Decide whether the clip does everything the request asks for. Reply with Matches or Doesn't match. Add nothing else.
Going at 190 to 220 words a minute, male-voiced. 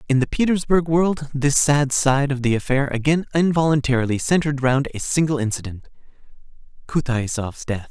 Doesn't match